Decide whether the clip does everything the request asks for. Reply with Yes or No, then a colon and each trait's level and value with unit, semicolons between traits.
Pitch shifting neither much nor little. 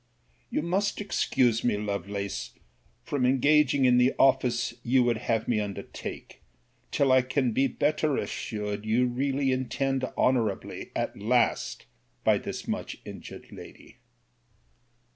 Yes: average, 3.3 semitones